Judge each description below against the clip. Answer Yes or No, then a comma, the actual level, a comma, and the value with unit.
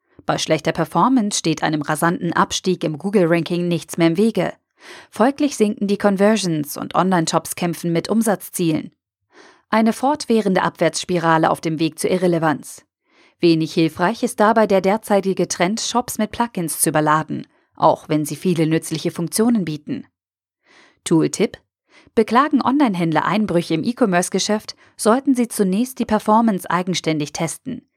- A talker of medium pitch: Yes, medium, 180 Hz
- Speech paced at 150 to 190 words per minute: No, average, 135 wpm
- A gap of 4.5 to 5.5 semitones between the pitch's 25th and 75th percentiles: Yes, average, 4.9 semitones